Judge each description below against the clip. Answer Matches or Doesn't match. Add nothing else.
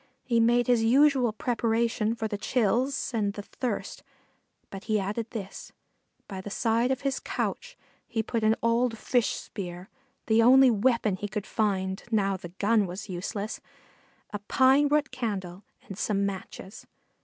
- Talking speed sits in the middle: Matches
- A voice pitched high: Matches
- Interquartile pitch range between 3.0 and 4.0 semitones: Matches